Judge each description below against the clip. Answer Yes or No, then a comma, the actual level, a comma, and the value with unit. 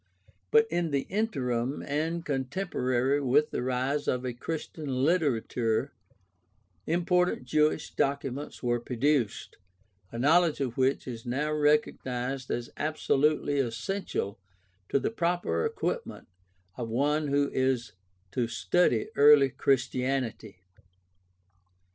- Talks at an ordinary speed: No, slow, 110 wpm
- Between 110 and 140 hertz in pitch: Yes, low, 135 Hz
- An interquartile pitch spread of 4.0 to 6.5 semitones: No, average, 3.5 semitones